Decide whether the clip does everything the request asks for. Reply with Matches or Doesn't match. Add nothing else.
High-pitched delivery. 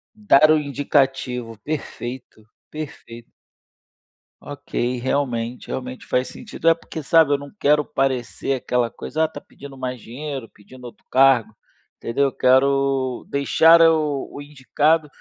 Doesn't match